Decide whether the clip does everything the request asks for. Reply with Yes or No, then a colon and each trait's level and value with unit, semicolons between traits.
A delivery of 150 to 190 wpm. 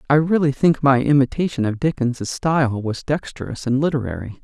Yes: average, 160 wpm